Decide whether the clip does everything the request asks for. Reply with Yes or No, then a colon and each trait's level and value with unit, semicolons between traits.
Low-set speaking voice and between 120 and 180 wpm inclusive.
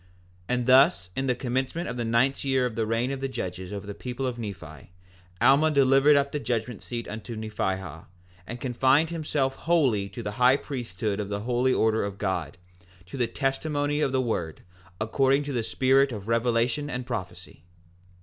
No: low, 125 Hz; average, 190 wpm